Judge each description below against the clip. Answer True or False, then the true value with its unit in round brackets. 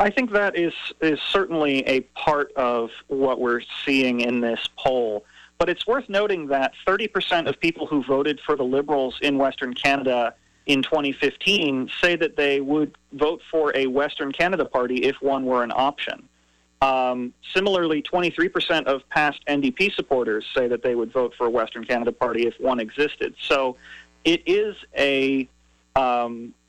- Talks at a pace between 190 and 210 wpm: False (165 wpm)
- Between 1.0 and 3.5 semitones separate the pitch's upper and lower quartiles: False (4.3 semitones)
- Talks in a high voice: False (140 Hz)